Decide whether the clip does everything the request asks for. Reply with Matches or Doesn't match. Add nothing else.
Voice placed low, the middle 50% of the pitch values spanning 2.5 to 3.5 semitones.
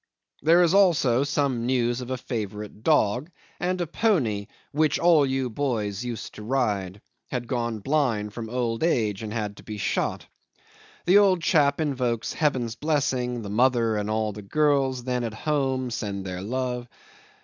Doesn't match